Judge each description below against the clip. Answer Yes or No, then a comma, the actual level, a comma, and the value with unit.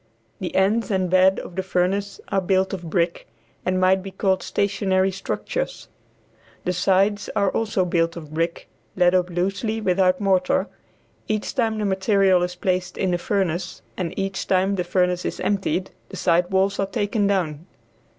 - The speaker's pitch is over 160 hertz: Yes, high, 190 Hz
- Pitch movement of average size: No, narrow, 1.6 semitones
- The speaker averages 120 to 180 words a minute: Yes, average, 170 wpm